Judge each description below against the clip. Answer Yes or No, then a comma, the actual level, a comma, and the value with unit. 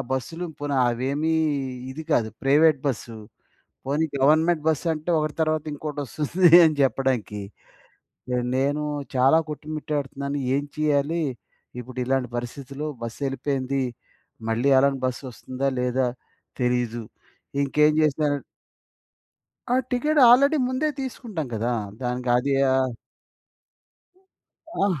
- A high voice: No, medium, 140 Hz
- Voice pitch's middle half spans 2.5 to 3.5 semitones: Yes, average, 3.2 semitones